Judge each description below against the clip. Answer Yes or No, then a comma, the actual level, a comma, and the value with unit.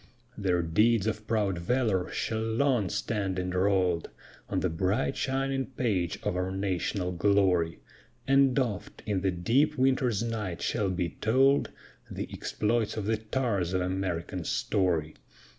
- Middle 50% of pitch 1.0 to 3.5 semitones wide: No, average, 4.3 semitones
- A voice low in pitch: Yes, low, 100 Hz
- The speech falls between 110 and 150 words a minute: Yes, average, 140 wpm